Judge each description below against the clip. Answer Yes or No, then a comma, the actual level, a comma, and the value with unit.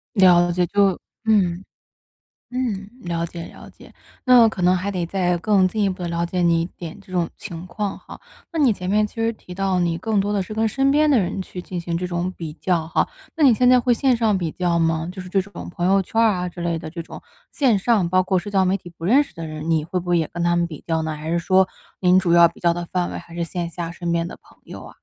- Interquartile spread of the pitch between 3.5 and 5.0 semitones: No, average, 2.9 semitones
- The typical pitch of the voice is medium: Yes, medium, 180 Hz